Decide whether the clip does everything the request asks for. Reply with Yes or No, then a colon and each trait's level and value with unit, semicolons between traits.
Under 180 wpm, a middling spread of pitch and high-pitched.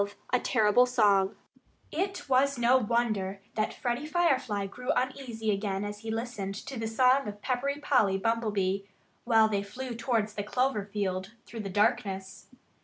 Yes: average, 160 wpm; average, 3.7 semitones; high, 225 Hz